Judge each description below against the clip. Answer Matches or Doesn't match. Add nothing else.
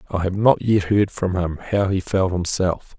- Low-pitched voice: Matches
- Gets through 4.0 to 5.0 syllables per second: Matches